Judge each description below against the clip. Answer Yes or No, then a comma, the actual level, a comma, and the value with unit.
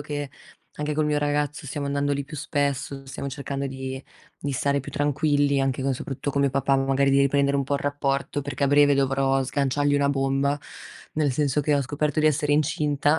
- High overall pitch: No, medium, 140 Hz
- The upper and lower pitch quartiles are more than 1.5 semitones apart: No, narrow, 1.1 semitones